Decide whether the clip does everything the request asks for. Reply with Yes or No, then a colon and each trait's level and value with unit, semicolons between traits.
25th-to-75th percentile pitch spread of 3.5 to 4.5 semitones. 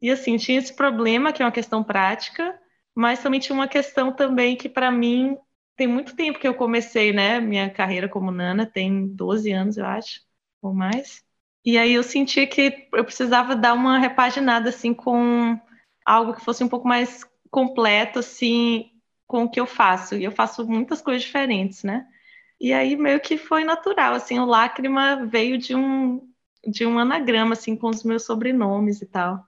No: average, 2.8 semitones